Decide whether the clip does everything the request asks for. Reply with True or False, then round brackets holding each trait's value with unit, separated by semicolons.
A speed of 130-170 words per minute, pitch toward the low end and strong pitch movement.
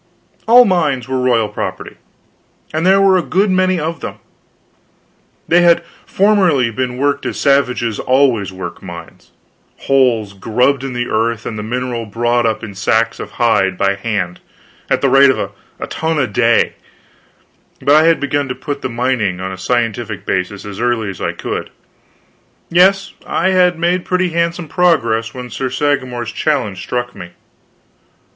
True (165 wpm; 125 Hz; 6.2 semitones)